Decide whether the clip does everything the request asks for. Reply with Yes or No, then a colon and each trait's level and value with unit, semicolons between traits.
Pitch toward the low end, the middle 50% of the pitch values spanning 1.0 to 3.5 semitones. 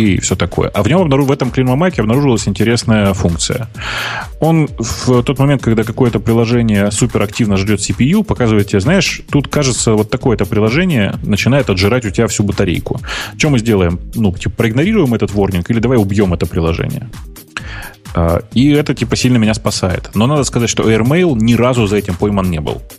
No: low, 115 Hz; average, 4.1 semitones